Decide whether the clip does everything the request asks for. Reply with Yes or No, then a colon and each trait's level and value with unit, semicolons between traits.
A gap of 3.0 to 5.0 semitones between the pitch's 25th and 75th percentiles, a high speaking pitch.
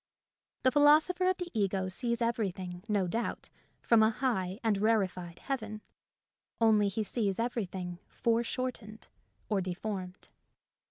Yes: average, 3.9 semitones; high, 215 Hz